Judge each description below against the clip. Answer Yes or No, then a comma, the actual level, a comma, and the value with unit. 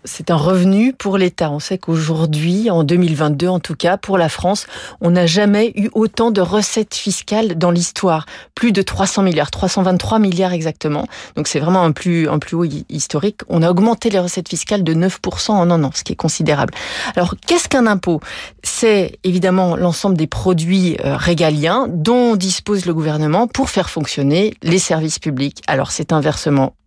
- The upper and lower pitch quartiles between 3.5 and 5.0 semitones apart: Yes, average, 3.8 semitones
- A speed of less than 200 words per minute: Yes, average, 180 wpm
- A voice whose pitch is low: No, medium, 180 Hz